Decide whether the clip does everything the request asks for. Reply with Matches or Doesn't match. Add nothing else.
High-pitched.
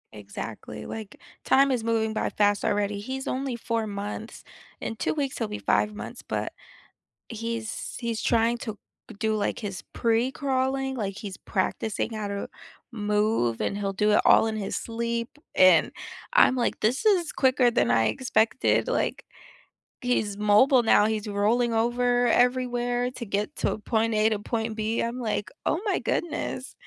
Matches